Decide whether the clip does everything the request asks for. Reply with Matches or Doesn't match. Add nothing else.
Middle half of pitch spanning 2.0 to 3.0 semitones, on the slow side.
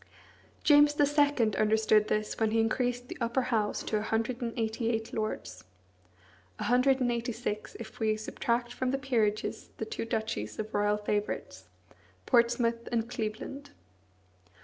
Doesn't match